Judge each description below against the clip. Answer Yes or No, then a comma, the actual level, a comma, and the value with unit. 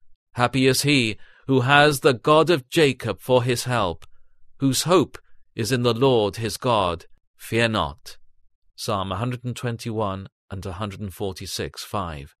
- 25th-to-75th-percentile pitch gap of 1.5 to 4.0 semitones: No, average, 5.2 semitones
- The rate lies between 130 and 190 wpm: Yes, average, 170 wpm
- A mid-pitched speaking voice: No, low, 115 Hz